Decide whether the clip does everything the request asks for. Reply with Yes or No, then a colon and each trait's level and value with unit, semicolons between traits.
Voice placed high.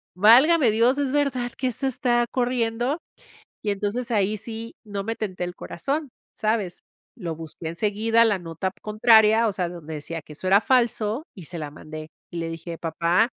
Yes: high, 215 Hz